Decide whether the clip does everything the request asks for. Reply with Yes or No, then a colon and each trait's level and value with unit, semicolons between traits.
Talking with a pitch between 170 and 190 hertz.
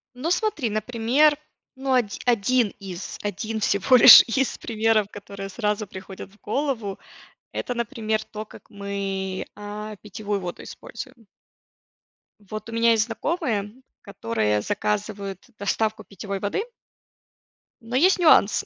No: high, 215 Hz